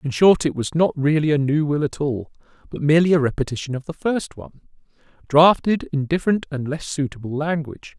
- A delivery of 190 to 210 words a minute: Yes, average, 195 wpm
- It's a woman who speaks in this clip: No, male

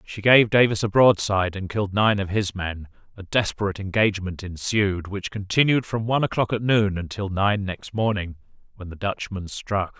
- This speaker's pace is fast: No, average, 180 wpm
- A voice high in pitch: No, low, 100 Hz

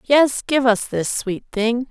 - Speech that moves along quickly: No, average, 190 wpm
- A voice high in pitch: Yes, high, 240 Hz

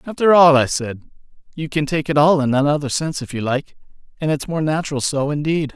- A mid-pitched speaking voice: Yes, medium, 150 Hz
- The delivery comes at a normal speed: No, fast, 220 wpm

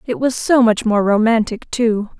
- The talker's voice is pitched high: Yes, high, 225 Hz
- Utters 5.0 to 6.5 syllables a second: No, 4.5 syllables/s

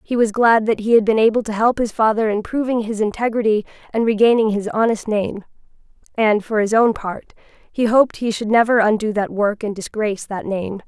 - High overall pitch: Yes, high, 220 Hz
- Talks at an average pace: No, fast, 210 wpm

